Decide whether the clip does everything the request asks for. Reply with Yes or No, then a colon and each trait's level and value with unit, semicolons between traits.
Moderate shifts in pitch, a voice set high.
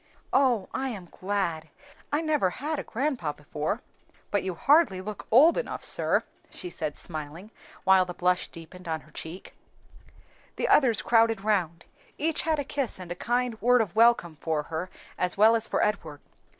No: wide, 6.4 semitones; high, 200 Hz